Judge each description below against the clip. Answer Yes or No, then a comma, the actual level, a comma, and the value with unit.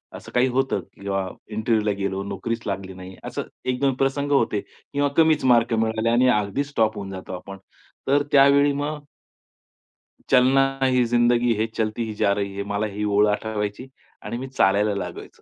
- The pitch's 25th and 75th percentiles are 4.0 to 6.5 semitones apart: Yes, average, 4.5 semitones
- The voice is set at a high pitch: No, low, 115 Hz